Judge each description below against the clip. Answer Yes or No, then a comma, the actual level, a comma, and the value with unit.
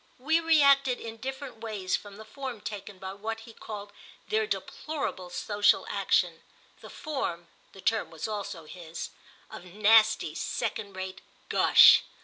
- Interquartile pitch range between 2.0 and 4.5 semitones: No, wide, 5.4 semitones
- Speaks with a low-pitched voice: No, high, 215 Hz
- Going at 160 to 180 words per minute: No, slow, 135 wpm